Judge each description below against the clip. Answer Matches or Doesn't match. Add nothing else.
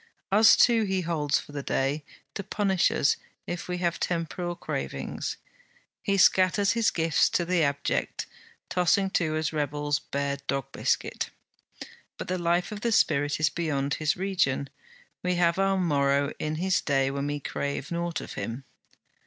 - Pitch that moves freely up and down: Doesn't match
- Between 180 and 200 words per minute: Doesn't match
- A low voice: Doesn't match